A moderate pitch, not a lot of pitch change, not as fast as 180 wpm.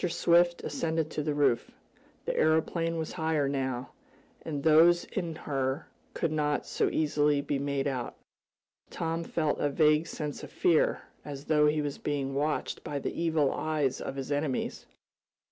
Yes: medium, 150 Hz; narrow, 2.2 semitones; average, 160 wpm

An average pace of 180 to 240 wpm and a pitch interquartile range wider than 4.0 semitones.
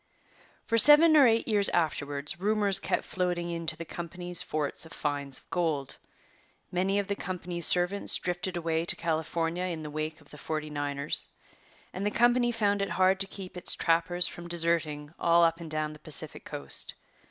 No: average, 185 wpm; average, 3.4 semitones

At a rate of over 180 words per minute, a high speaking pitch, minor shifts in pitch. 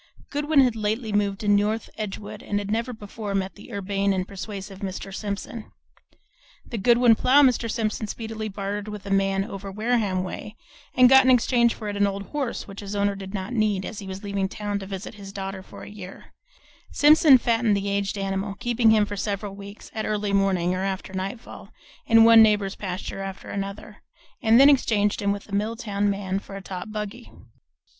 Yes: average, 195 wpm; high, 205 Hz; narrow, 2.2 semitones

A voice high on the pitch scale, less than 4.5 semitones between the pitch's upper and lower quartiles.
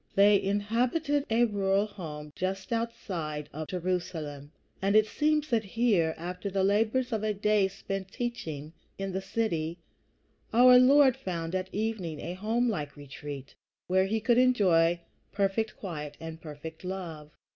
No: high, 195 Hz; average, 5.2 semitones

